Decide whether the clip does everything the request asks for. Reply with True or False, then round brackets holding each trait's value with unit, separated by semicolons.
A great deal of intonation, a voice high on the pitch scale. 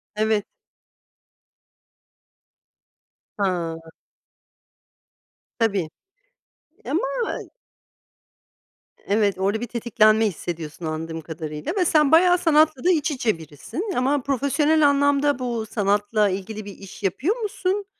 True (7.1 semitones; 220 Hz)